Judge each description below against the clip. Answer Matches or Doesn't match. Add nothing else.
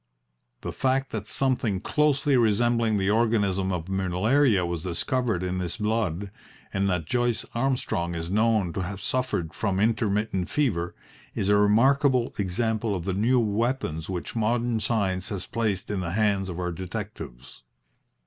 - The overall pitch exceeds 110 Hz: Doesn't match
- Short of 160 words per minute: Matches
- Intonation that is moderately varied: Matches